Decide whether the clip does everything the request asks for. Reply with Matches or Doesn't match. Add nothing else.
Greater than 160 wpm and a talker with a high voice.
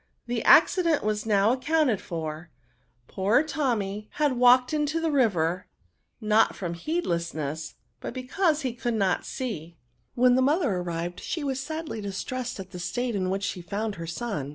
Matches